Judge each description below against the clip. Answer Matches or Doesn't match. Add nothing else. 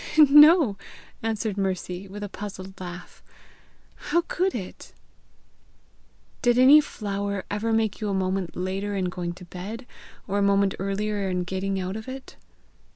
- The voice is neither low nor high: Doesn't match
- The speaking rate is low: Doesn't match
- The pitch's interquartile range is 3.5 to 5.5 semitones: Doesn't match